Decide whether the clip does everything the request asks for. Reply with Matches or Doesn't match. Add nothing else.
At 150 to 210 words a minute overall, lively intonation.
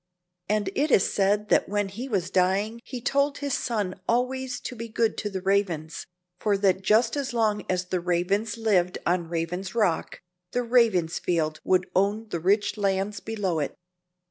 Doesn't match